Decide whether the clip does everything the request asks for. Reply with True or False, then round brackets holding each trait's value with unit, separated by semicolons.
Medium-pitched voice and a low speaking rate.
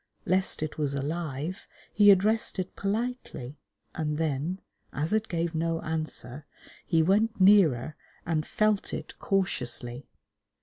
True (165 Hz; 125 wpm)